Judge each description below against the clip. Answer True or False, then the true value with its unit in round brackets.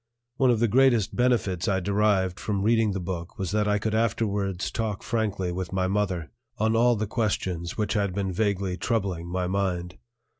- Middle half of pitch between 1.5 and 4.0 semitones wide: True (3.0 semitones)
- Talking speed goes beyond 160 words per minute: True (185 wpm)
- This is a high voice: False (100 Hz)